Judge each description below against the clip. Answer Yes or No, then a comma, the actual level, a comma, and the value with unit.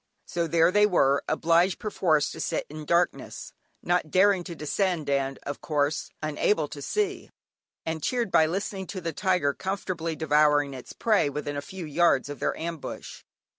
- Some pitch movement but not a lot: Yes, average, 4.1 semitones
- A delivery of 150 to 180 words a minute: Yes, average, 170 wpm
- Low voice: No, medium, 165 Hz